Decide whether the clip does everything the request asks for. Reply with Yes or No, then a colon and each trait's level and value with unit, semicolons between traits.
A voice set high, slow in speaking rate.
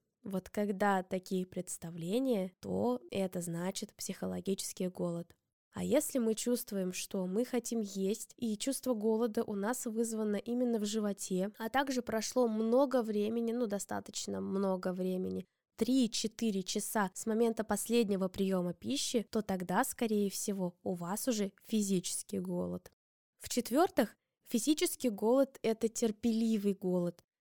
No: high, 210 Hz; average, 125 wpm